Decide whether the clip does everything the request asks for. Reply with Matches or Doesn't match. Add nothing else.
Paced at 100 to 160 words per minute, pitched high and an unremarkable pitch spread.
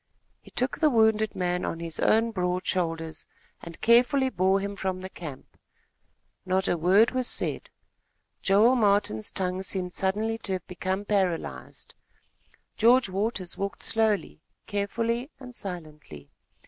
Matches